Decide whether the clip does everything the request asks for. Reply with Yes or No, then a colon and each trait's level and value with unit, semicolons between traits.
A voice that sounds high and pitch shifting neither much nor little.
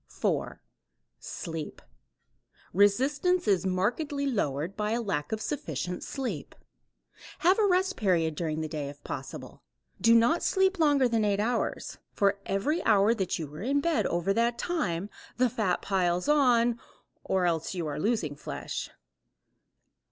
No: high, 210 Hz; wide, 7.4 semitones